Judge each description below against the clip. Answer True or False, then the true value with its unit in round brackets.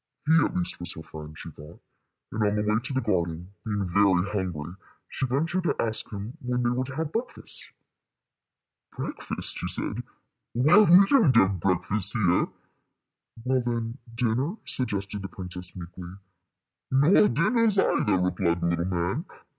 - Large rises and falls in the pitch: True (6.5 semitones)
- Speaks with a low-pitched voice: True (105 Hz)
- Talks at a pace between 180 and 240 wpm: False (160 wpm)